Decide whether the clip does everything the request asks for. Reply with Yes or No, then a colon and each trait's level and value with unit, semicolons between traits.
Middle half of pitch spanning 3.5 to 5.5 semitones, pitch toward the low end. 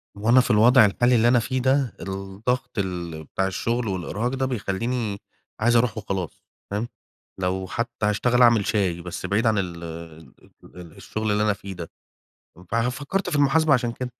Yes: average, 4.5 semitones; low, 110 Hz